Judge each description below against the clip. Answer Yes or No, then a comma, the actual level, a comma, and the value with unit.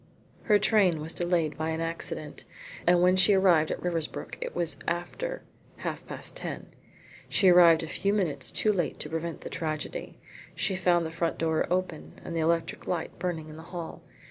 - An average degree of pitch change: No, narrow, 2.1 semitones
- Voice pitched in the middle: Yes, medium, 170 Hz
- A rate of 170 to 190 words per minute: Yes, average, 185 wpm